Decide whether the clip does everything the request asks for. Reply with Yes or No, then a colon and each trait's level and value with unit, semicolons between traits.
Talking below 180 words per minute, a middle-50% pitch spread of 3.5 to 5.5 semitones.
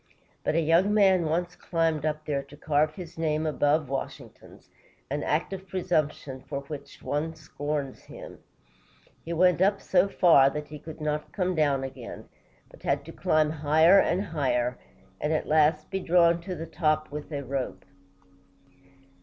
No: average, 170 wpm; narrow, 2.6 semitones